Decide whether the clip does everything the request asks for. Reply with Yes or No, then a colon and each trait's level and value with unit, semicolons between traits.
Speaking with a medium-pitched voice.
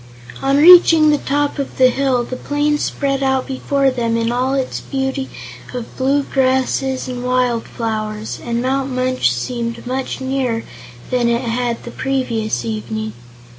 No: very high, 255 Hz